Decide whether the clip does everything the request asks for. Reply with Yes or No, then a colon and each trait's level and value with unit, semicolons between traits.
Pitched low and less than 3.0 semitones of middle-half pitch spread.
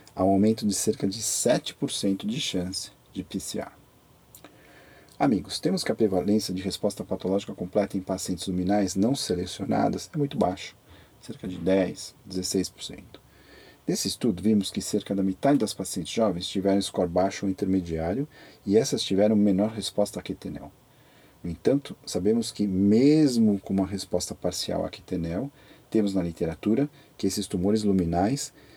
Yes: low, 100 Hz; narrow, 2.5 semitones